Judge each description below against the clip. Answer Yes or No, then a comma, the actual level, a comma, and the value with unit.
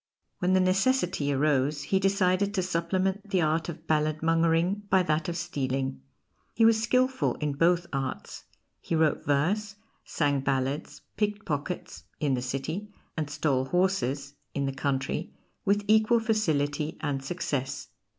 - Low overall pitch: No, medium, 165 Hz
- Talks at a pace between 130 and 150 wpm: Yes, average, 140 wpm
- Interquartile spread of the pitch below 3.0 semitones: No, average, 5.2 semitones